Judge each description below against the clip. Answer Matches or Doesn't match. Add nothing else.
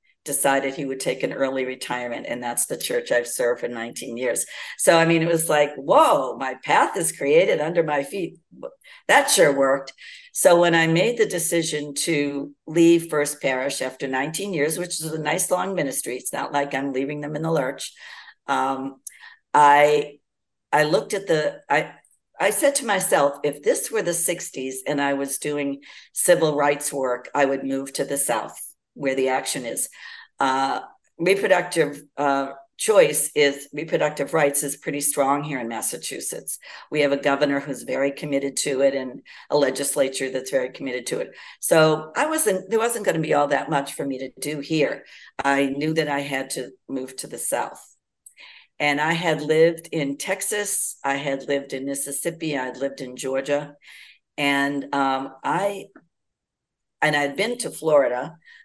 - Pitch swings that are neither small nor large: Matches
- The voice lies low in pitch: Doesn't match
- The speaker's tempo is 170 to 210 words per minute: Matches